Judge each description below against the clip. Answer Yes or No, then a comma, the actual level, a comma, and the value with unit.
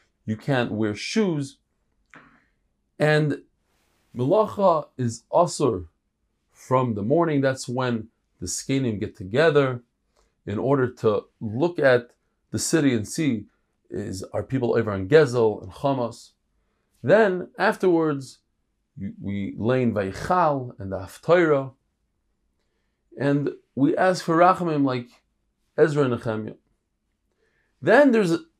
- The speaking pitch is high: No, low, 130 Hz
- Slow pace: Yes, slow, 110 wpm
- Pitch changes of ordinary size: No, wide, 5.8 semitones